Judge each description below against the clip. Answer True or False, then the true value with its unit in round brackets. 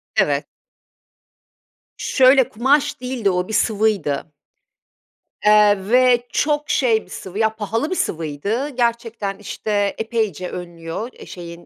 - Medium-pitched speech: False (220 Hz)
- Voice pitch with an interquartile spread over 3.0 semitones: True (4.5 semitones)